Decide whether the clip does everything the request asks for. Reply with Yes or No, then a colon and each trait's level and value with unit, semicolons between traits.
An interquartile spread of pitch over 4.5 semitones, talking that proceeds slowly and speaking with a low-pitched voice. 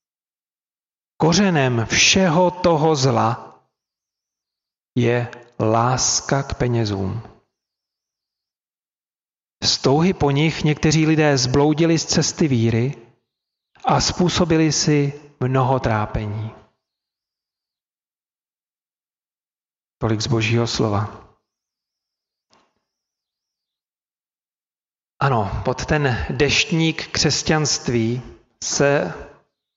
Yes: average, 5.3 semitones; slow, 65 wpm; low, 130 Hz